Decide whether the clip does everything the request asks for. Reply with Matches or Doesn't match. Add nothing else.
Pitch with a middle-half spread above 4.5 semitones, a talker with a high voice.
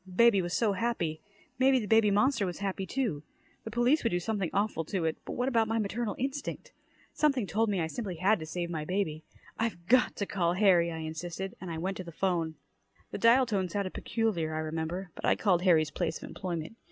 Matches